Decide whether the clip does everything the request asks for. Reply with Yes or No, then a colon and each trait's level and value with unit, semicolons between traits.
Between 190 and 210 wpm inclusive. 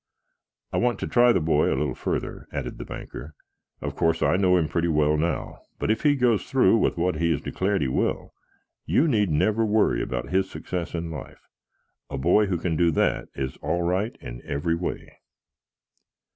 Yes: average, 195 wpm